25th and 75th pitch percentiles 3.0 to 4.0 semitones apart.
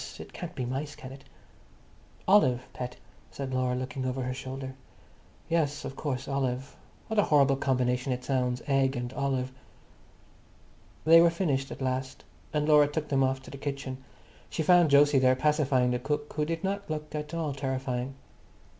No: narrow, 2.6 semitones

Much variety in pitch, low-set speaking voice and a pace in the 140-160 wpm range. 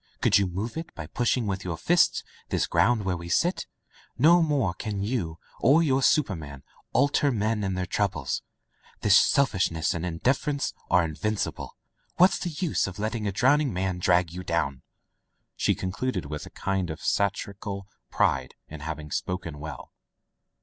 No: wide, 6.9 semitones; low, 100 Hz; average, 170 wpm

